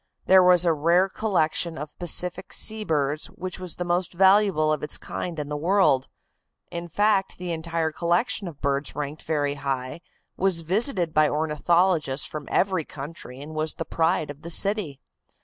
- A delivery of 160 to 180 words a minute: Yes, average, 170 wpm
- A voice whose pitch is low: No, medium, 165 Hz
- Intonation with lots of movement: No, average, 3.4 semitones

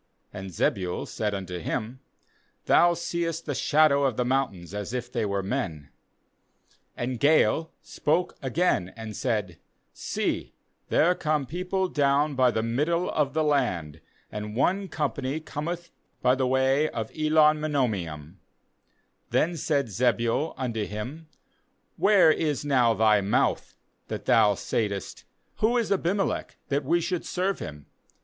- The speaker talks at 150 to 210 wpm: No, average, 140 wpm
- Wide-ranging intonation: Yes, wide, 6.7 semitones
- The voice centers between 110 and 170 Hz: Yes, low, 135 Hz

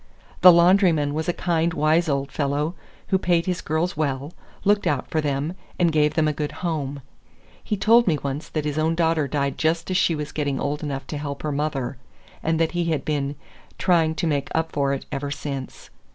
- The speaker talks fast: Yes, fast, 210 wpm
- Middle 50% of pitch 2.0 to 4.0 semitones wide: Yes, average, 2.8 semitones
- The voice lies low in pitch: No, medium, 155 Hz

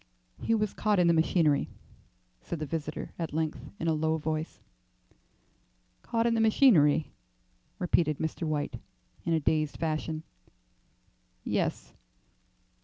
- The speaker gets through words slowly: Yes, slow, 125 wpm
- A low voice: No, medium, 160 Hz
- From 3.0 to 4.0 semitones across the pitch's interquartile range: No, narrow, 2.4 semitones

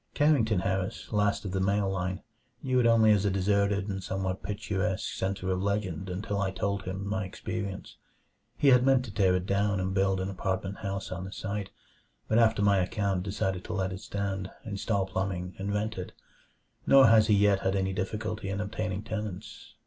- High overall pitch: No, low, 100 Hz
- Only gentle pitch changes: Yes, narrow, 1.8 semitones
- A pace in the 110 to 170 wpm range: No, average, 195 wpm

